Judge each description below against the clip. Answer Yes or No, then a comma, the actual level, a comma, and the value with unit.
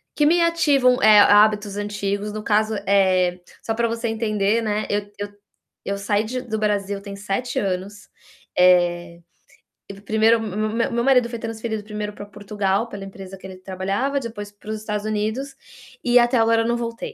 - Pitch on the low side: No, high, 210 Hz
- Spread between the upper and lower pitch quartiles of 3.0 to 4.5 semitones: No, narrow, 2.4 semitones